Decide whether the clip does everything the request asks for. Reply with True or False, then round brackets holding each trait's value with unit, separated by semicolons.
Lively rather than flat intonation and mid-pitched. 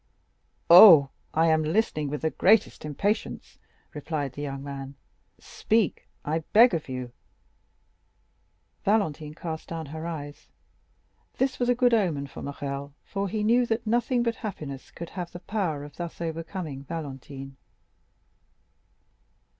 True (6.2 semitones; 160 Hz)